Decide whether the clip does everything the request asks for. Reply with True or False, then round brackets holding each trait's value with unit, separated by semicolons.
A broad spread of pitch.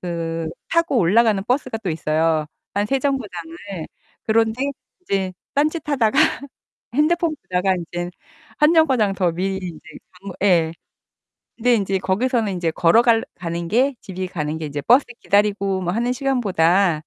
True (6.1 semitones)